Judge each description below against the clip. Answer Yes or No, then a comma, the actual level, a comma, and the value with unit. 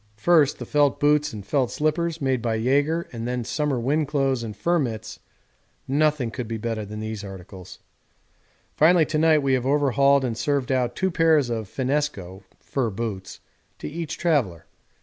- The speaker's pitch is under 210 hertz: Yes, low, 135 Hz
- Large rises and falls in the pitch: No, average, 4.8 semitones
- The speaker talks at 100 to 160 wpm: No, average, 170 wpm